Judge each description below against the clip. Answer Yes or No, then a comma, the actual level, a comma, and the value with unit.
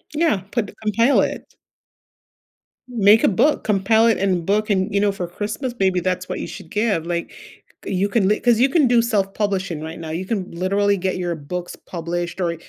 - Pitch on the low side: No, high, 195 Hz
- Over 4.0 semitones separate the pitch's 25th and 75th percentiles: No, average, 3.4 semitones